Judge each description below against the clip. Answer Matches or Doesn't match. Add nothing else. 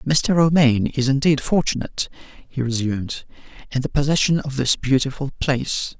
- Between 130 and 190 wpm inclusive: Matches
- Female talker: Doesn't match